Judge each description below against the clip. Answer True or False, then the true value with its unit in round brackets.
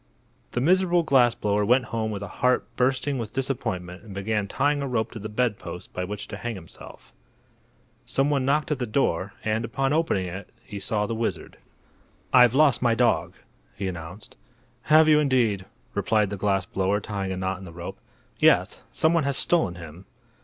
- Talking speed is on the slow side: False (190 wpm)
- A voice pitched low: True (110 Hz)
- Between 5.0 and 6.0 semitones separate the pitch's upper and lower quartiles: True (5.4 semitones)